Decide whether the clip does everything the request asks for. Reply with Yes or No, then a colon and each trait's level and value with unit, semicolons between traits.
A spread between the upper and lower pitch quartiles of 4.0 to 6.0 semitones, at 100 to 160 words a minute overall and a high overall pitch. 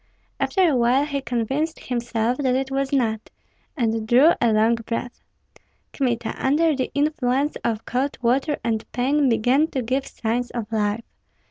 No: average, 3.2 semitones; average, 155 wpm; very high, 250 Hz